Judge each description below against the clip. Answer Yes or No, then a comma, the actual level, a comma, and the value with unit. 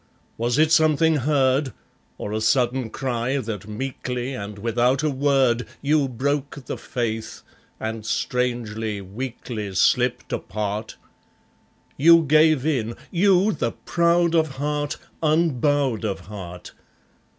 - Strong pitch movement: No, average, 4.9 semitones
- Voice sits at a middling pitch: No, low, 130 Hz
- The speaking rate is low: Yes, slow, 115 wpm